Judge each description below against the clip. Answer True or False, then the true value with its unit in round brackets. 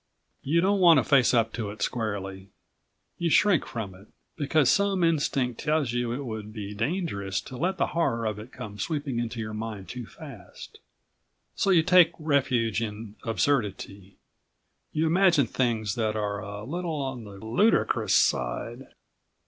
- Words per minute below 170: True (160 wpm)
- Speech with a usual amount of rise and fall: False (6.6 semitones)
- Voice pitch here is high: False (120 Hz)